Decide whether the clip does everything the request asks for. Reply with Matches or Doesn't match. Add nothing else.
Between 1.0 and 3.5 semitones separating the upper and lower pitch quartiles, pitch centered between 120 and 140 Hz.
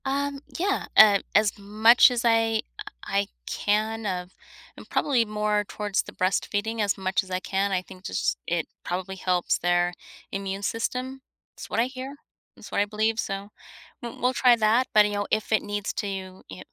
Doesn't match